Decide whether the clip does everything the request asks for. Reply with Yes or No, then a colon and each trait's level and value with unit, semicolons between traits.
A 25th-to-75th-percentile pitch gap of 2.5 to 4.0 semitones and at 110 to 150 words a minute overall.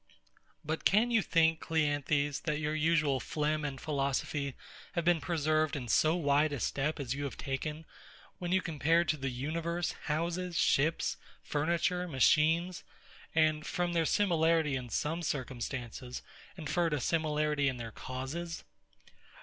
Yes: average, 2.9 semitones; average, 140 wpm